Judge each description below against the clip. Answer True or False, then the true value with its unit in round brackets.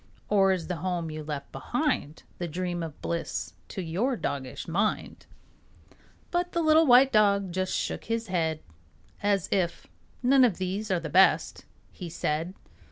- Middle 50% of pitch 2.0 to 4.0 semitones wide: False (4.6 semitones)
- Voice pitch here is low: False (185 Hz)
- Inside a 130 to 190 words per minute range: True (155 wpm)